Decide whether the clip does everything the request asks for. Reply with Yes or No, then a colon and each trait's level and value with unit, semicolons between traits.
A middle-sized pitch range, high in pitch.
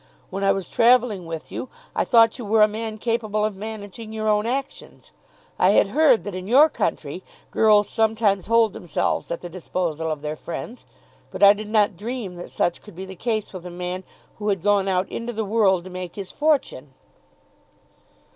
Yes: average, 3.4 semitones; high, 205 Hz